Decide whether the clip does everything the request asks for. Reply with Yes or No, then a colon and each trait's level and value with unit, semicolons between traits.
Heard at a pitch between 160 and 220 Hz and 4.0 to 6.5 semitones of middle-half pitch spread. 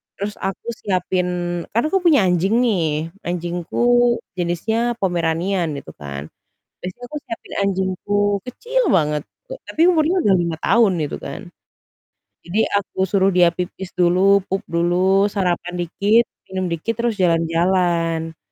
No: medium, 185 Hz; average, 3.3 semitones